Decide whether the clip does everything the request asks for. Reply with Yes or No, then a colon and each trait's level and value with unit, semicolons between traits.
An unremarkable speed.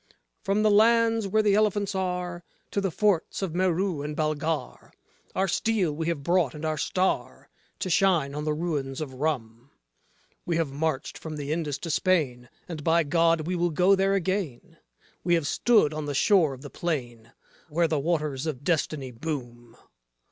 Yes: average, 175 wpm